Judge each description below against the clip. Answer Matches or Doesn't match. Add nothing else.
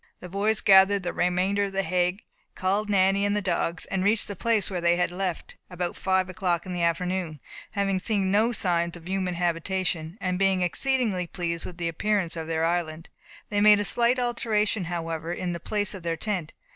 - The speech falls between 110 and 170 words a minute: Doesn't match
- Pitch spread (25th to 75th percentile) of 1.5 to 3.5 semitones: Matches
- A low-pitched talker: Doesn't match